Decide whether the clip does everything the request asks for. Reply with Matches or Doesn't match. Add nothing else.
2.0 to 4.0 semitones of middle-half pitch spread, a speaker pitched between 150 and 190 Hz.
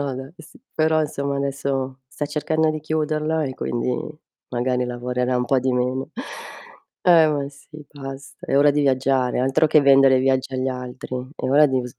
Doesn't match